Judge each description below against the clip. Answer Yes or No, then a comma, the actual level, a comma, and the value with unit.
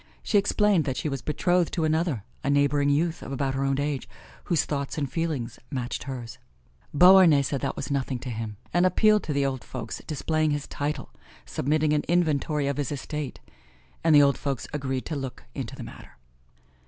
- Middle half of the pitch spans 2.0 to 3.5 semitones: Yes, average, 2.7 semitones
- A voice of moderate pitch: Yes, medium, 145 Hz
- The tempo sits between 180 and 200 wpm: Yes, average, 190 wpm